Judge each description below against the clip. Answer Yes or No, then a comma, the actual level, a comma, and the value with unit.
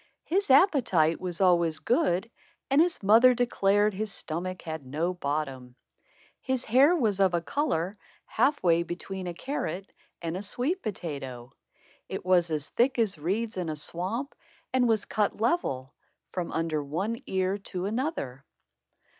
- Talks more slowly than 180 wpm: Yes, average, 150 wpm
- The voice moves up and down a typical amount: No, wide, 6.1 semitones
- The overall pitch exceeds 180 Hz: Yes, high, 190 Hz